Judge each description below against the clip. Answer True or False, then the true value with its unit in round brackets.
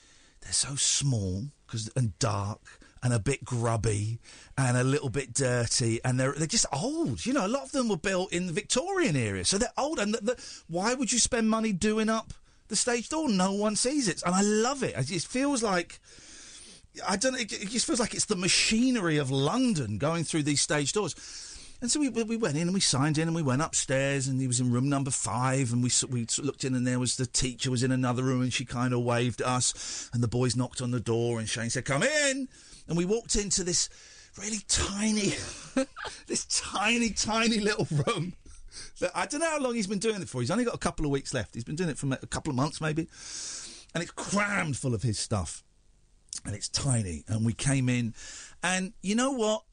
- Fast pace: True (230 wpm)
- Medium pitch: True (150 Hz)